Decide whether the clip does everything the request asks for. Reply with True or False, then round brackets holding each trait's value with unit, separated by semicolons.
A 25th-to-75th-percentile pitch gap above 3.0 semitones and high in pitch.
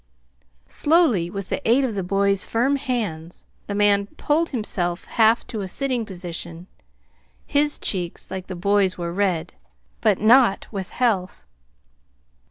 True (4.8 semitones; 200 Hz)